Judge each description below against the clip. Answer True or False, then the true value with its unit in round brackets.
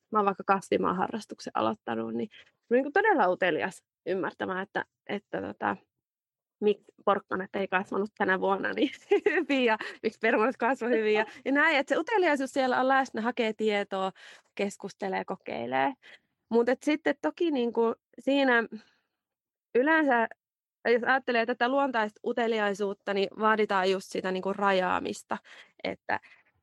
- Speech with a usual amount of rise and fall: True (4.8 semitones)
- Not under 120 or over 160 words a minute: True (135 wpm)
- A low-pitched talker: False (225 Hz)